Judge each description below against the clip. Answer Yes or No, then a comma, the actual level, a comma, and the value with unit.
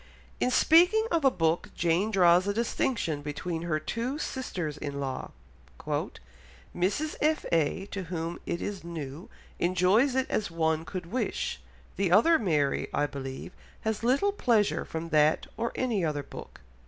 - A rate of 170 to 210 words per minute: No, average, 155 wpm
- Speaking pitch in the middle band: Yes, medium, 180 Hz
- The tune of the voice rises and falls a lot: Yes, wide, 6.5 semitones